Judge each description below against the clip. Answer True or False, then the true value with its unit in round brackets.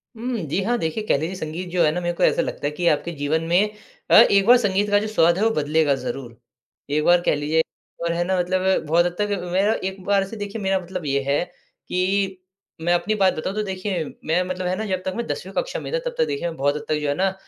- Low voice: False (185 Hz)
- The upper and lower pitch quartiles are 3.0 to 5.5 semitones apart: True (3.9 semitones)